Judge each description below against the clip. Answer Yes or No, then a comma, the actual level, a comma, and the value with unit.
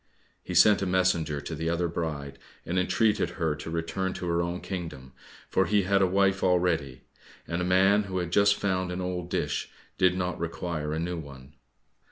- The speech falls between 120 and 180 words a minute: No, average, 195 wpm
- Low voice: Yes, very low, 90 Hz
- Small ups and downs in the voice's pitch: Yes, narrow, 2.3 semitones